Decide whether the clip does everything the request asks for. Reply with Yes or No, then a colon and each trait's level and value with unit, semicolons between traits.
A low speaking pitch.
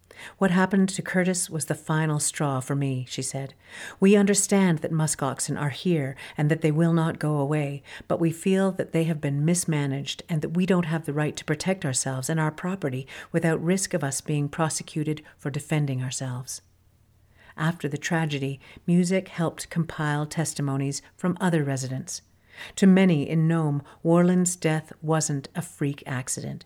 No: medium, 155 Hz